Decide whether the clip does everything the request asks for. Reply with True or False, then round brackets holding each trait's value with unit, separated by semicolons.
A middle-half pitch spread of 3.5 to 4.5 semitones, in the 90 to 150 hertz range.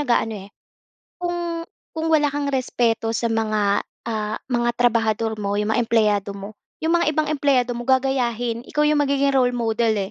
False (4.2 semitones; 240 Hz)